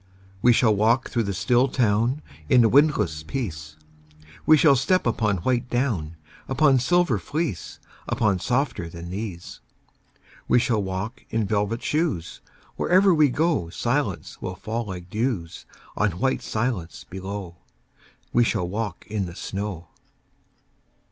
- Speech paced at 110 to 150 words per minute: Yes, slow, 135 wpm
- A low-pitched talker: Yes, low, 110 Hz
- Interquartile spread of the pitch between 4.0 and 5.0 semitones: No, wide, 5.6 semitones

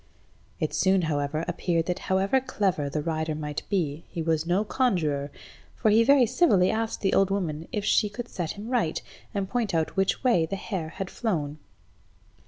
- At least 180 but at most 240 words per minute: Yes, average, 185 wpm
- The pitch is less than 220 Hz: Yes, high, 190 Hz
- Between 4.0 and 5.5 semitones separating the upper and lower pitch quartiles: Yes, average, 5.0 semitones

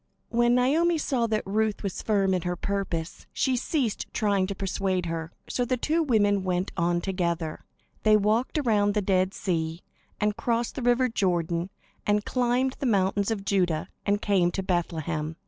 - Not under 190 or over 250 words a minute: No, average, 170 wpm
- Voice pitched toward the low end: No, high, 200 Hz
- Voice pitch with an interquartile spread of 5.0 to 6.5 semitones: No, average, 4.6 semitones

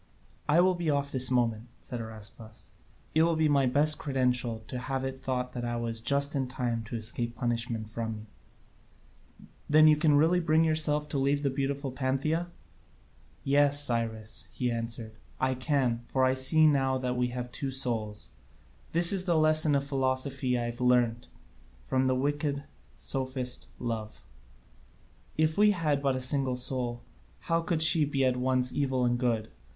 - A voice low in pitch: Yes, low, 130 Hz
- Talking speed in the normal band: Yes, average, 170 wpm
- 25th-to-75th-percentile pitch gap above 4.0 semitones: No, average, 3.2 semitones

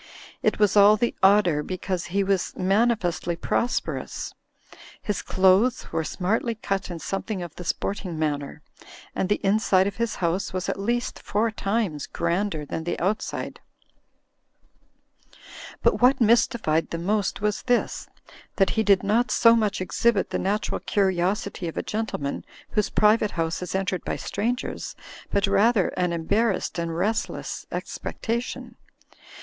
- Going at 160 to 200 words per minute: No, average, 145 wpm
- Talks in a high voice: Yes, high, 195 Hz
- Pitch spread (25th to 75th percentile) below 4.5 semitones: Yes, average, 3.4 semitones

